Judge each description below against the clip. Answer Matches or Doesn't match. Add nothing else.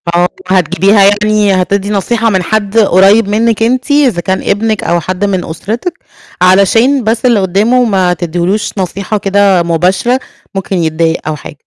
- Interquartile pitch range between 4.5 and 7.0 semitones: Doesn't match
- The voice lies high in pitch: Matches